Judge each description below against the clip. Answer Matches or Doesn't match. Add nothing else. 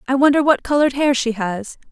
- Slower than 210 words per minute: Doesn't match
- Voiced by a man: Doesn't match